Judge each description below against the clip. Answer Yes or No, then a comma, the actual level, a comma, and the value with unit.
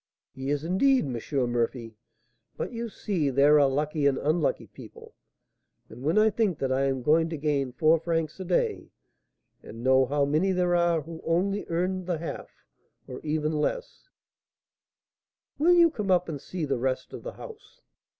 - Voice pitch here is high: No, medium, 155 Hz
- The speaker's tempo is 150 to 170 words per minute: No, average, 180 wpm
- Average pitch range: Yes, average, 5.0 semitones